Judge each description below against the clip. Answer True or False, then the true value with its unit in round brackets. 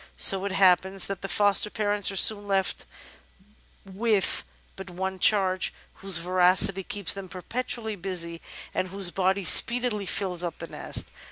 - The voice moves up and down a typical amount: False (1.7 semitones)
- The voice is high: True (195 Hz)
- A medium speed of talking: True (150 wpm)